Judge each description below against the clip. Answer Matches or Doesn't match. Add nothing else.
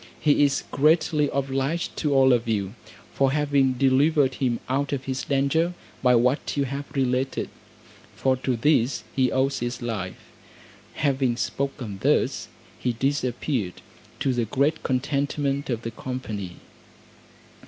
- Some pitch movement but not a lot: Doesn't match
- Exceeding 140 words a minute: Doesn't match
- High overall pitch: Doesn't match